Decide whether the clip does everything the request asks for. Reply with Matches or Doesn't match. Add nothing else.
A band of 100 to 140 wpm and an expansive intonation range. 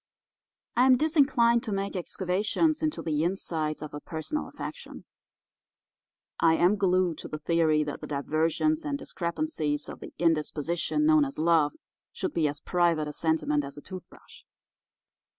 Doesn't match